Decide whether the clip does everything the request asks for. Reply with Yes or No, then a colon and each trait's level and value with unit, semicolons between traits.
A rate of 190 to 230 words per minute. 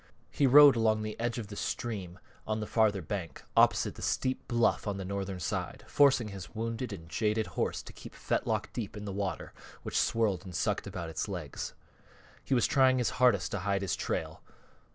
Yes: average, 195 wpm